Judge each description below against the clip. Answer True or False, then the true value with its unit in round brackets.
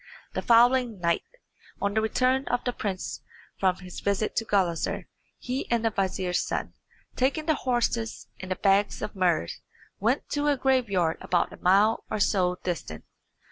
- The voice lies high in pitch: True (210 Hz)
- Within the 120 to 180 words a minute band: True (160 wpm)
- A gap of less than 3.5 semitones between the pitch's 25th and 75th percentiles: False (4.9 semitones)